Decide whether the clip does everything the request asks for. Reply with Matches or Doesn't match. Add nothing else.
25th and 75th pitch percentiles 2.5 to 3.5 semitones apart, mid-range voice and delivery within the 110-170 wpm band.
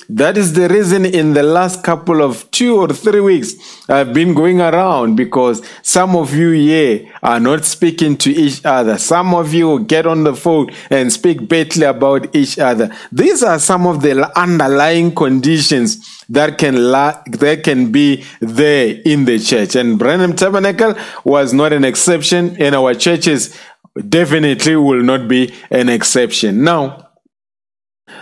Doesn't match